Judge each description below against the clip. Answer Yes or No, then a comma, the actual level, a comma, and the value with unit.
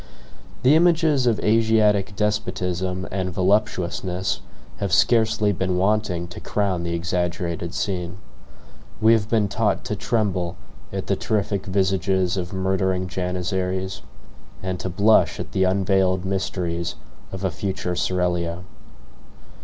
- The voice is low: Yes, very low, 95 Hz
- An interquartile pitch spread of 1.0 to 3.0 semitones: Yes, narrow, 2.4 semitones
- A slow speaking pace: Yes, slow, 120 wpm